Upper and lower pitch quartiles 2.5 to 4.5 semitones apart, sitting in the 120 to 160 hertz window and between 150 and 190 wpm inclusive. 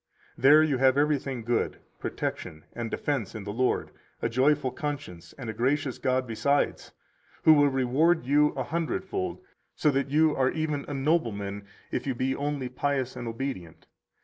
Yes: average, 3.5 semitones; low, 135 Hz; average, 170 wpm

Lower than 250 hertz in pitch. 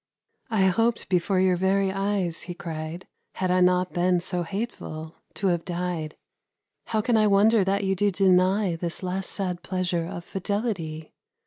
Yes: medium, 185 Hz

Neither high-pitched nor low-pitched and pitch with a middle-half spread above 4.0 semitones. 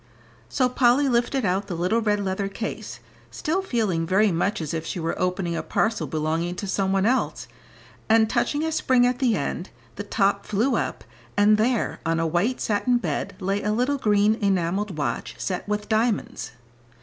No: high, 205 Hz; average, 4.5 semitones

